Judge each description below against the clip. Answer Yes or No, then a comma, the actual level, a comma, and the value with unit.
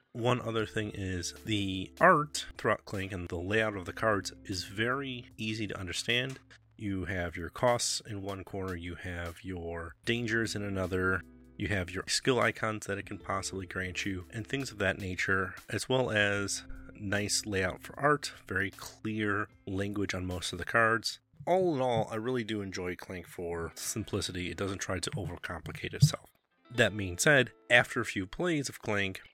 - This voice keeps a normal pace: Yes, average, 180 wpm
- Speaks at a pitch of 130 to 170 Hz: No, low, 100 Hz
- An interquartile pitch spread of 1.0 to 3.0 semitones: No, average, 3.6 semitones